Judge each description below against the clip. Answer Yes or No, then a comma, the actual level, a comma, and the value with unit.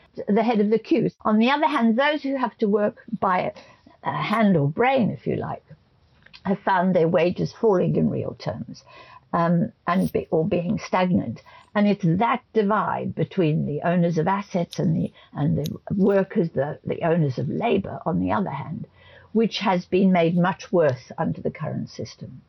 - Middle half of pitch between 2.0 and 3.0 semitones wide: No, average, 4.3 semitones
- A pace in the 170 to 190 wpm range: Yes, average, 180 wpm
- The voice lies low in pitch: No, high, 195 Hz